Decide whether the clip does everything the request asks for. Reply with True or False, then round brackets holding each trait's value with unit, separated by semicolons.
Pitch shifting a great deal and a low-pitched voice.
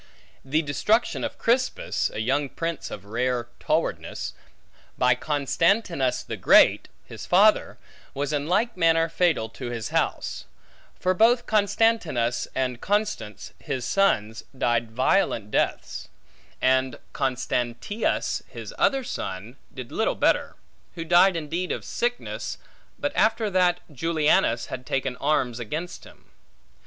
False (7.0 semitones; 145 Hz)